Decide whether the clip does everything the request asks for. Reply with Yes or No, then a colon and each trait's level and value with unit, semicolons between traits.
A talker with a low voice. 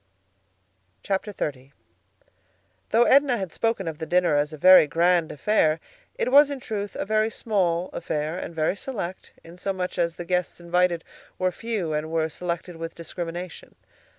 No: medium, 180 Hz